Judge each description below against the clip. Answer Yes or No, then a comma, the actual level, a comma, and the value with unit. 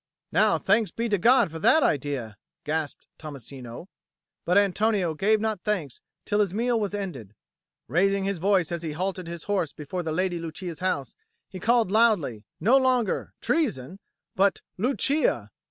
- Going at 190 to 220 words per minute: No, average, 155 wpm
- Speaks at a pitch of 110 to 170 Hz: No, medium, 185 Hz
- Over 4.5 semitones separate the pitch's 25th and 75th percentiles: Yes, average, 5.1 semitones